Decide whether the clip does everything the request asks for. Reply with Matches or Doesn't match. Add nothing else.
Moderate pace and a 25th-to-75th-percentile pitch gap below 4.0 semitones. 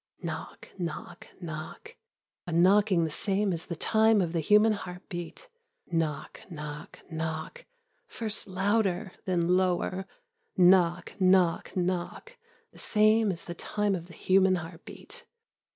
Doesn't match